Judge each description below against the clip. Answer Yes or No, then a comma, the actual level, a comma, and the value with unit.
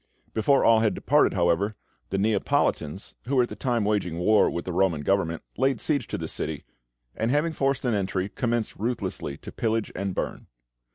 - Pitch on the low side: Yes, low, 105 Hz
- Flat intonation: No, average, 4.6 semitones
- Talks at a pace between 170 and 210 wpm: Yes, average, 185 wpm